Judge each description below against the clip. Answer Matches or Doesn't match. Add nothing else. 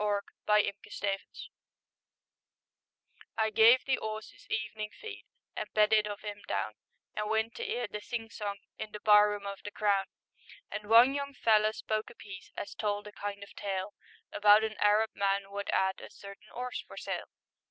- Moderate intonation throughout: Doesn't match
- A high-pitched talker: Matches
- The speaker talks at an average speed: Matches